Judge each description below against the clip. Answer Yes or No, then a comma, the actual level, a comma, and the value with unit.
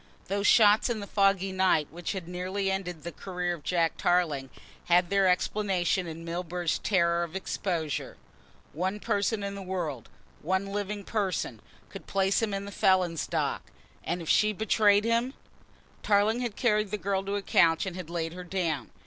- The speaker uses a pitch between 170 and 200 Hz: Yes, high, 190 Hz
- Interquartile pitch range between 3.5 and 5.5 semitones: No, average, 2.7 semitones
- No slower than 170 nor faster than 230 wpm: Yes, average, 175 wpm